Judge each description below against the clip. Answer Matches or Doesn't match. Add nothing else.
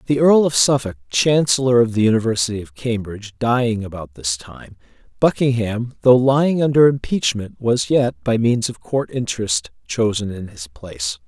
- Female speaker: Doesn't match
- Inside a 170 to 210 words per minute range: Doesn't match